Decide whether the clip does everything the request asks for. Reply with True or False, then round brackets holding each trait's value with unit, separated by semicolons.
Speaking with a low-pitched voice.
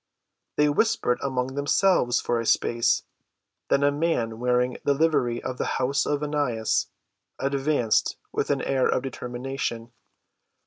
True (130 Hz)